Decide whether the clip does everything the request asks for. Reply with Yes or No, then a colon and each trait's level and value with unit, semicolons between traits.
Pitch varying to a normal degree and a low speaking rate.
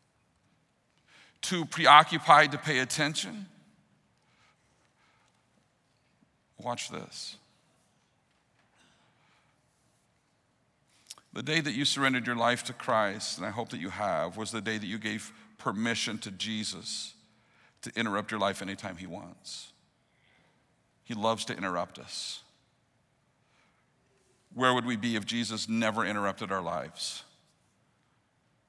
Yes: average, 3.9 semitones; slow, 110 wpm